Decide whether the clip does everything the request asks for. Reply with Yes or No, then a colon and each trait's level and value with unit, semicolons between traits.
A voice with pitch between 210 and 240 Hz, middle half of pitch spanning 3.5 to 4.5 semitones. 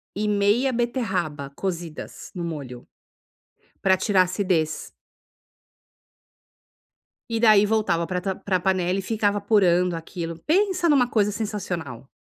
No: high, 190 Hz; average, 3.9 semitones